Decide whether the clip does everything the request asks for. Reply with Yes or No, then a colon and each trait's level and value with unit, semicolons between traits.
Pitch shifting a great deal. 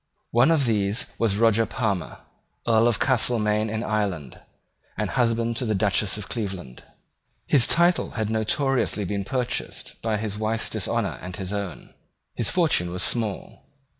No: average, 2.7 semitones